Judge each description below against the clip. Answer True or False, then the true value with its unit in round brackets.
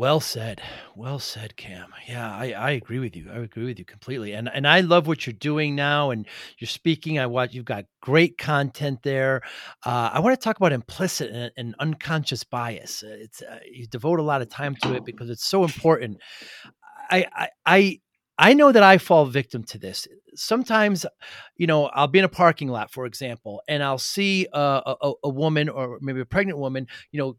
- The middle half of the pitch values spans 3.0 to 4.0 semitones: False (4.8 semitones)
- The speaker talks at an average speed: False (210 wpm)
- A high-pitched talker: False (135 Hz)